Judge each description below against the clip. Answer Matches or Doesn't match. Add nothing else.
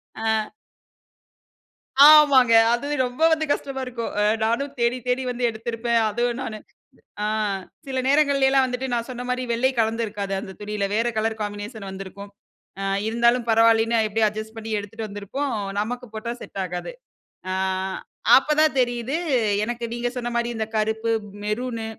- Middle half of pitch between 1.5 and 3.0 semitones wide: Matches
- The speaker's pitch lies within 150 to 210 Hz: Doesn't match